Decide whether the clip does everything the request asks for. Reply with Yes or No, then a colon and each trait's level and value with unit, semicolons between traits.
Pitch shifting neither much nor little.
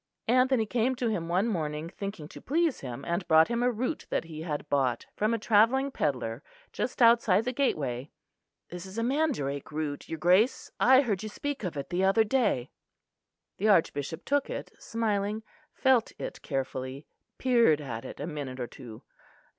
No: wide, 8.0 semitones